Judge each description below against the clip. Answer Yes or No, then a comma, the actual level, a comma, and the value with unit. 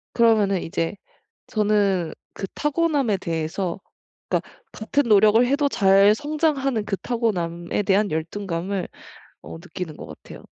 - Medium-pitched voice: No, high, 205 Hz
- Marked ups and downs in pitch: No, average, 4.8 semitones